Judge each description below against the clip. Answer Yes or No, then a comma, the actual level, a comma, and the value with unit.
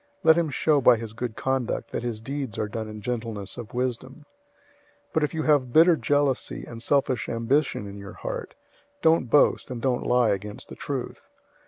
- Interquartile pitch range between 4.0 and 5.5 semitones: Yes, average, 4.3 semitones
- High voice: No, low, 125 Hz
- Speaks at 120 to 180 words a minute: No, average, 190 wpm